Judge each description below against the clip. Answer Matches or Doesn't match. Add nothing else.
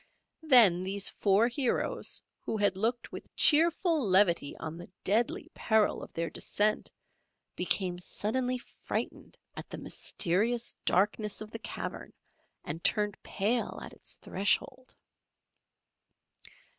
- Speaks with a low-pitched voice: Doesn't match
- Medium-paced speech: Doesn't match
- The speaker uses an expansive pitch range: Doesn't match